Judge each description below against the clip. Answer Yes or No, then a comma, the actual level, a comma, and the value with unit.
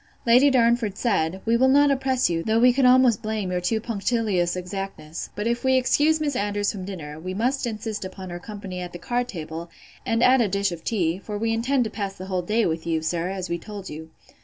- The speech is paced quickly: Yes, fast, 235 wpm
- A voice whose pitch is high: Yes, high, 205 Hz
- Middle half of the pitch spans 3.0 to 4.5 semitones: No, average, 4.9 semitones